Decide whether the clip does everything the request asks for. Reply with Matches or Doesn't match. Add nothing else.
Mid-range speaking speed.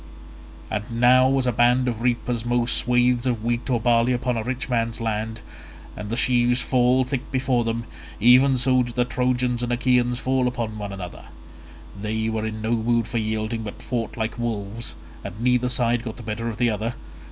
Matches